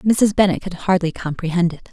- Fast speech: No, average, 190 wpm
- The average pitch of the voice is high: No, medium, 180 Hz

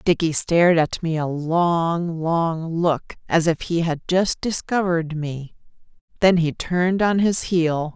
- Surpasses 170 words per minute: No, average, 160 wpm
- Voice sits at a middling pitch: Yes, medium, 170 Hz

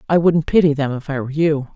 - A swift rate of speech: Yes, fast, 275 wpm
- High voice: No, medium, 150 Hz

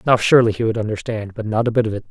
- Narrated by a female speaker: No, male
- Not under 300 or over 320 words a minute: Yes, fast, 315 wpm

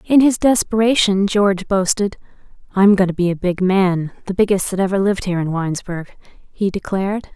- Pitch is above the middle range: Yes, high, 195 Hz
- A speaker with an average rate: Yes, average, 180 wpm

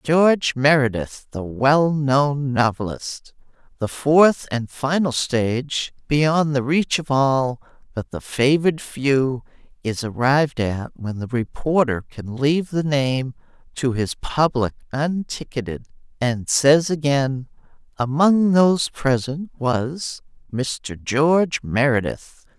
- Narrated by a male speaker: No, female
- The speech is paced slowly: Yes, slow, 115 wpm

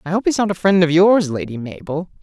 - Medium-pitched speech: Yes, medium, 180 Hz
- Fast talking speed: Yes, fast, 270 wpm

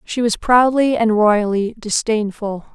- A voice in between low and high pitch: No, high, 220 Hz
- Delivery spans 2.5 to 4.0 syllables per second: Yes, 3.9 syllables/s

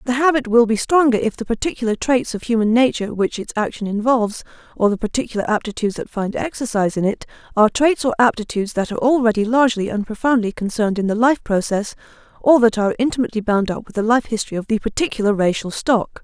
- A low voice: No, high, 225 Hz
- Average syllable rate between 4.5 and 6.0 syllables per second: No, 6.7 syllables/s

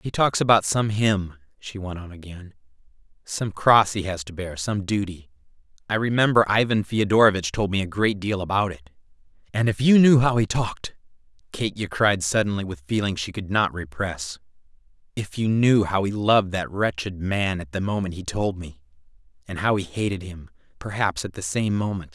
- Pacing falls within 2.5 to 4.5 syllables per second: No, 5.1 syllables/s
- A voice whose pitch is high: No, low, 100 Hz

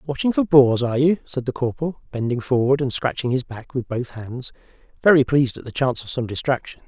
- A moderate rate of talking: No, fast, 220 wpm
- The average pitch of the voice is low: Yes, low, 130 Hz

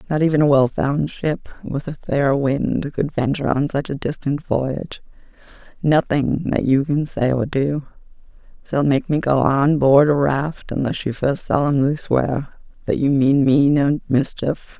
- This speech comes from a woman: Yes, female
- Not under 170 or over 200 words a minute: Yes, average, 175 wpm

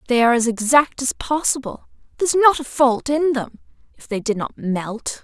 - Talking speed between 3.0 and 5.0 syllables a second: No, 5.3 syllables/s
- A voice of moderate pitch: No, very high, 255 Hz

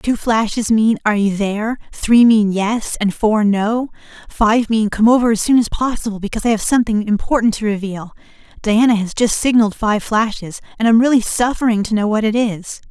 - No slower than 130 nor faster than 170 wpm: No, average, 195 wpm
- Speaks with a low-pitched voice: No, high, 220 Hz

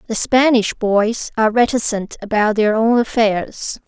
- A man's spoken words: No, female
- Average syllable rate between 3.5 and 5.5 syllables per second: Yes, 4.3 syllables/s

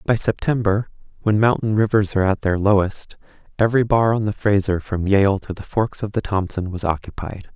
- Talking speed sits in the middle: Yes, average, 190 wpm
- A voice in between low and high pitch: No, low, 100 Hz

